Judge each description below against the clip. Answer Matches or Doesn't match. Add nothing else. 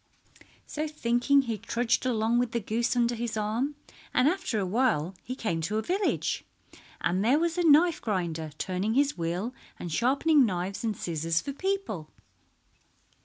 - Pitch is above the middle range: Matches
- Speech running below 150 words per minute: Doesn't match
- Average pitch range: Doesn't match